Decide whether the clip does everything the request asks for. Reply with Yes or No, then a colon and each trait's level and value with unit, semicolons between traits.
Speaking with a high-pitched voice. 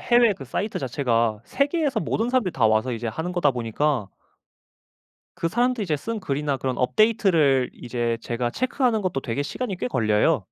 No: medium, 145 Hz